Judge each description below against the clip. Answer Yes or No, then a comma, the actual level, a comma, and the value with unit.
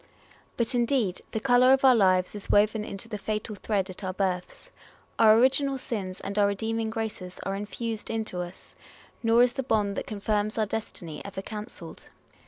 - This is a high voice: Yes, high, 215 Hz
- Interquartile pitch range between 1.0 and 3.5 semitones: Yes, average, 2.7 semitones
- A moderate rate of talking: Yes, average, 180 wpm